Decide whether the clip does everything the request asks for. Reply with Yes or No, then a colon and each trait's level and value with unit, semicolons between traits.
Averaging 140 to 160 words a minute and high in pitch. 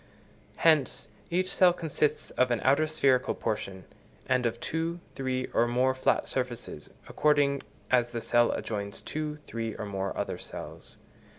No: average, 150 wpm; low, 130 Hz